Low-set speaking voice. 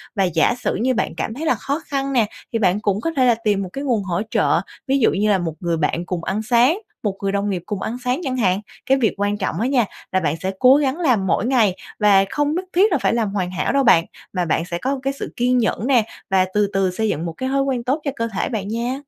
No: high, 220 Hz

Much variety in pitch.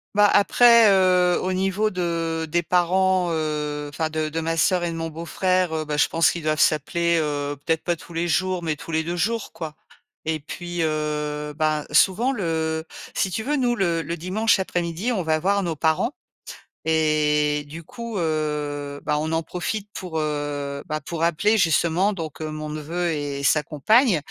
No: average, 3.2 semitones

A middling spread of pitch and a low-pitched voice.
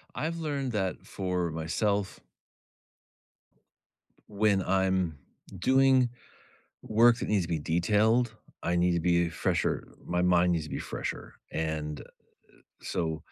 Yes: average, 4.3 semitones; very low, 95 Hz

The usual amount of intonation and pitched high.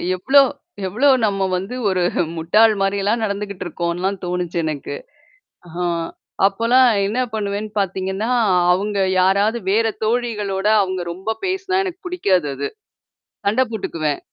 Yes: average, 3.4 semitones; high, 200 Hz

